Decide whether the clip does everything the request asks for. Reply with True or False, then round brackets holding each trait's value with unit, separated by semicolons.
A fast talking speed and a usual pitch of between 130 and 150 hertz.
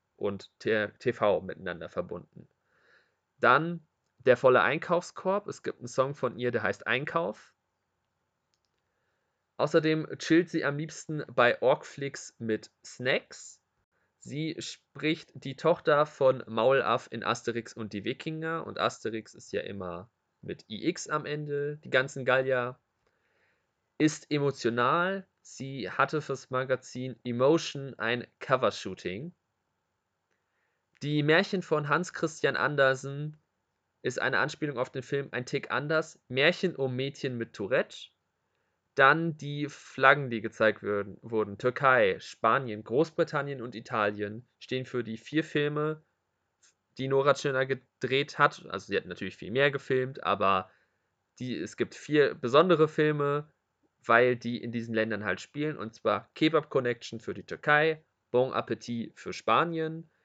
False (130 wpm; 135 Hz)